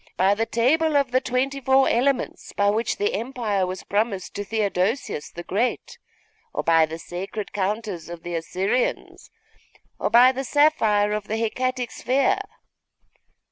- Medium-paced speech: Yes, average, 150 wpm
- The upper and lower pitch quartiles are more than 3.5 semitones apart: Yes, average, 4.7 semitones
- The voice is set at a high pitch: Yes, high, 220 Hz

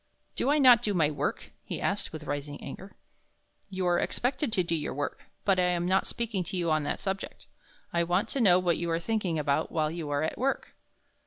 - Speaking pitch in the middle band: Yes, medium, 175 Hz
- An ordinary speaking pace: No, fast, 225 wpm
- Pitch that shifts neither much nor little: Yes, average, 4.1 semitones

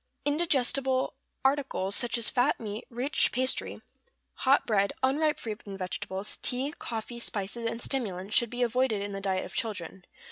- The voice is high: Yes, high, 235 Hz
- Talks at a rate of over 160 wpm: No, average, 155 wpm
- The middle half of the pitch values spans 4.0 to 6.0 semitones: Yes, average, 4.5 semitones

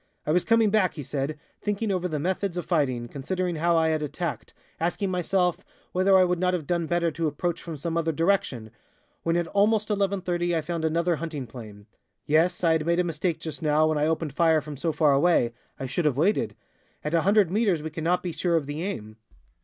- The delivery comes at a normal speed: No, fast, 215 wpm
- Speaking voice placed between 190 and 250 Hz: No, medium, 165 Hz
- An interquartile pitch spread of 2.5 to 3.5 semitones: Yes, average, 3.0 semitones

